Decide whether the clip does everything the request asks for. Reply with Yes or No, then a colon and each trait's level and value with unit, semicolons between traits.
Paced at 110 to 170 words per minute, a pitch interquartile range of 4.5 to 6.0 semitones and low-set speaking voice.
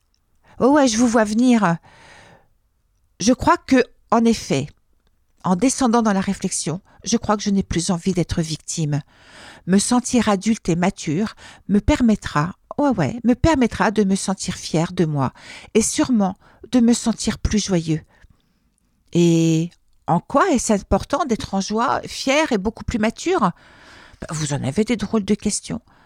No: average, 160 wpm; wide, 5.5 semitones; high, 210 Hz